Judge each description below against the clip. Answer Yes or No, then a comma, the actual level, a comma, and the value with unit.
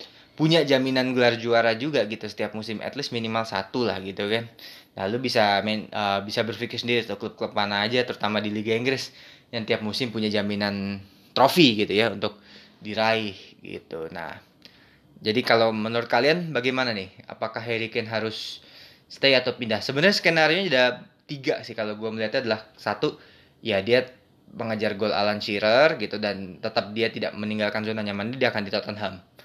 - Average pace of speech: No, fast, 175 wpm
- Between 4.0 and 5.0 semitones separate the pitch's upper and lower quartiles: No, average, 2.9 semitones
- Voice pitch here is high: No, low, 110 Hz